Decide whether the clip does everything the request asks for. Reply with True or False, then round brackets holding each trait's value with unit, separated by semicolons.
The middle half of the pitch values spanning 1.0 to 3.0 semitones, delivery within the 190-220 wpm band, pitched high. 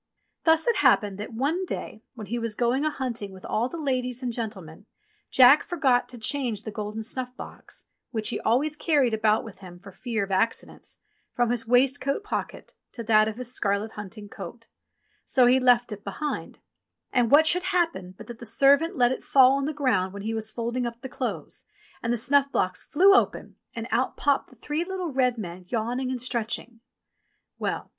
False (3.9 semitones; 205 wpm; 240 Hz)